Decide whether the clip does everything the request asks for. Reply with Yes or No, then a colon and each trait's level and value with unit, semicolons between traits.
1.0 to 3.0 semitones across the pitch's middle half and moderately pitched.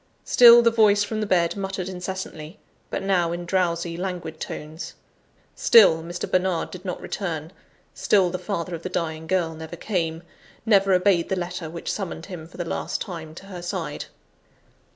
Yes: narrow, 2.5 semitones; medium, 180 Hz